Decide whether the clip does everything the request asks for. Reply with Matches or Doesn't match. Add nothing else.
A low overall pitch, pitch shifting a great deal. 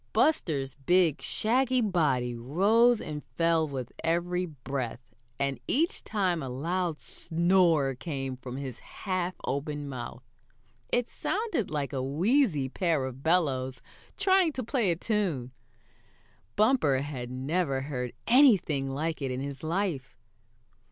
Doesn't match